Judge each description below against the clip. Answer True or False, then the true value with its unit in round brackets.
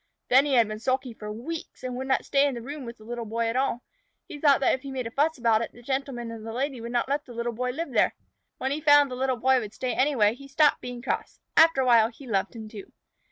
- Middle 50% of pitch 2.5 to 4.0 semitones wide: True (3.0 semitones)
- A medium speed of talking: False (285 wpm)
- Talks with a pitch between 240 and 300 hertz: True (250 Hz)